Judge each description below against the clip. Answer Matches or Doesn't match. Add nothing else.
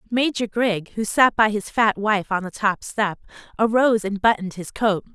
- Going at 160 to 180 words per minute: Doesn't match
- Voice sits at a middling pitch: Doesn't match